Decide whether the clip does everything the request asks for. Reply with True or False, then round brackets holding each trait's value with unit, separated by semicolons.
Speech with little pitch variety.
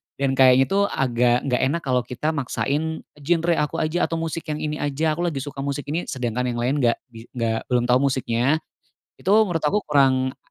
False (3.7 semitones)